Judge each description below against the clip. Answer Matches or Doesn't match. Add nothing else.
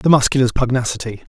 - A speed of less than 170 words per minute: Matches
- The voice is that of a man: Matches